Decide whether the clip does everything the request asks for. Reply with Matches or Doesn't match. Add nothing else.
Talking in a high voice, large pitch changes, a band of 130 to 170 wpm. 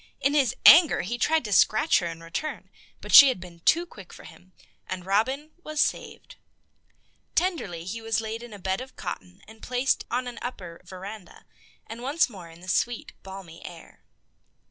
Doesn't match